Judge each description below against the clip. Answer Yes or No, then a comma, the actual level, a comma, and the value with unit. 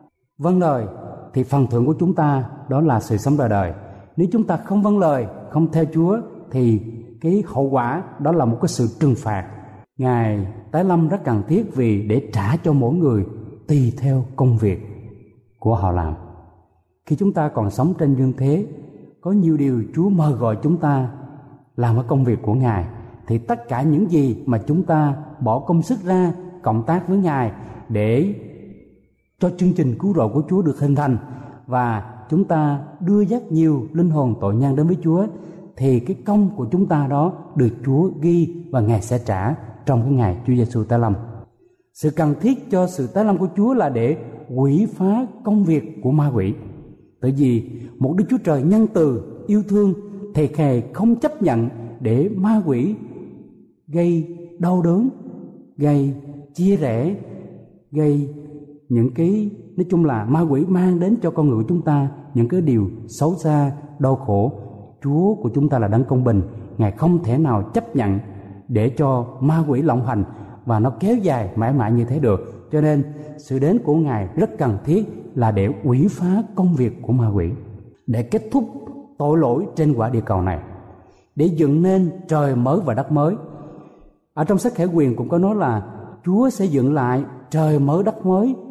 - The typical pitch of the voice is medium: Yes, medium, 145 Hz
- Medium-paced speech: Yes, average, 190 wpm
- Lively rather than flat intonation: Yes, wide, 6.5 semitones